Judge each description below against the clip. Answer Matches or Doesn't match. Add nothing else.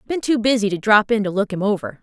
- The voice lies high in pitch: Matches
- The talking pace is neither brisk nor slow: Doesn't match